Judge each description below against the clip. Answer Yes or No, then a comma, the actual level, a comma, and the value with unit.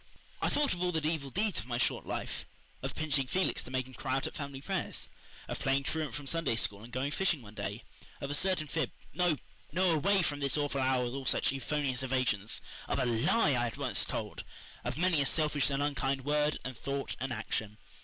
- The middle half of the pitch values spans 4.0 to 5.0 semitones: No, average, 3.3 semitones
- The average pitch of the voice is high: No, medium, 140 Hz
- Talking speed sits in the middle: No, fast, 225 wpm